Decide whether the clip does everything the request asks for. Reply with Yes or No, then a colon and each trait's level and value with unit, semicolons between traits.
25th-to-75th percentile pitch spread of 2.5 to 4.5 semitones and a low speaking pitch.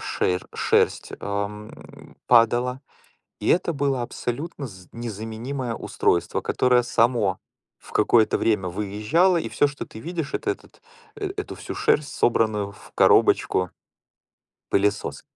No: average, 5.2 semitones; low, 115 Hz